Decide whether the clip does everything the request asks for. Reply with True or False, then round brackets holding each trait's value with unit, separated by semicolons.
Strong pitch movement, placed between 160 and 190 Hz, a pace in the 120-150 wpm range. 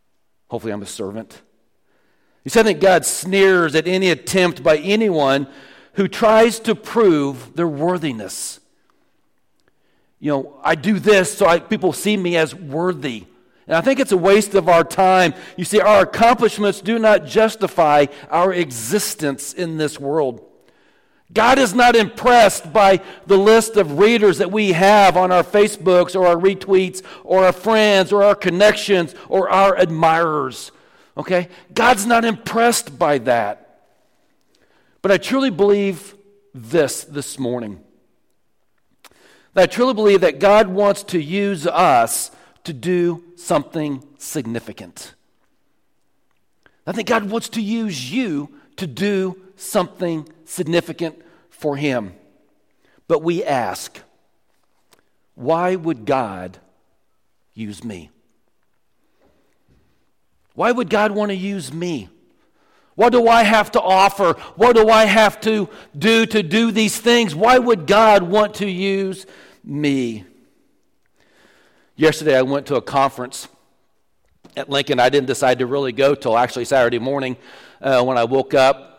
True (5.7 semitones; 185 Hz; 140 wpm)